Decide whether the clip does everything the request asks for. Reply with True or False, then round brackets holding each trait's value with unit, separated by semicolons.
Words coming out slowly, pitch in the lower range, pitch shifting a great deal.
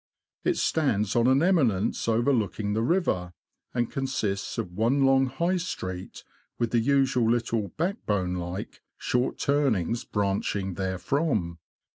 True (130 wpm; 115 Hz; 5.7 semitones)